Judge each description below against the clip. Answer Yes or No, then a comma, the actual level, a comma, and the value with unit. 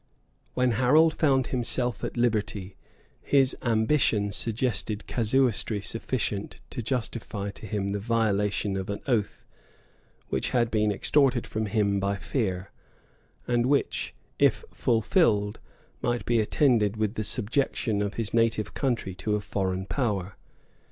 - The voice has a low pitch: Yes, low, 110 Hz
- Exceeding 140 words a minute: No, slow, 135 wpm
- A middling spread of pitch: Yes, average, 3.2 semitones